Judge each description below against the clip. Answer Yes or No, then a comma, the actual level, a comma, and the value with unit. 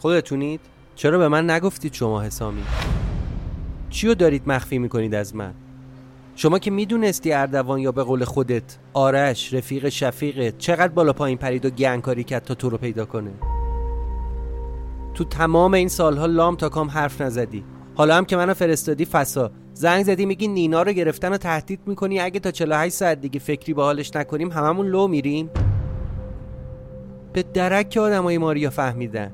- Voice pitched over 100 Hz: Yes, medium, 140 Hz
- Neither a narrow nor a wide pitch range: No, wide, 6.0 semitones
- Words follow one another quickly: Yes, fast, 160 wpm